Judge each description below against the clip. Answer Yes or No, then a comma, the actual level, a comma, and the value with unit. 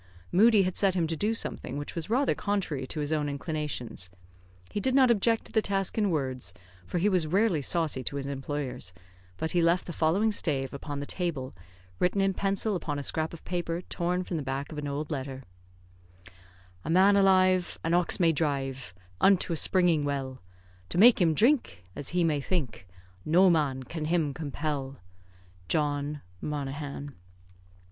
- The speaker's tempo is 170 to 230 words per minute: Yes, average, 180 wpm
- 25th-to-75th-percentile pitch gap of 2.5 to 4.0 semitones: No, average, 4.6 semitones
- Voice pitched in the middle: Yes, medium, 160 Hz